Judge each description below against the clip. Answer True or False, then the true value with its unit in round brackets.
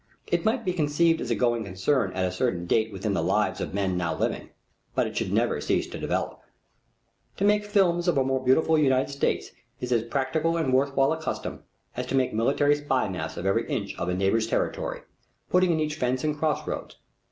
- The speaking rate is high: True (220 wpm)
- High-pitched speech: False (130 Hz)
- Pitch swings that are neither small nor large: False (7.0 semitones)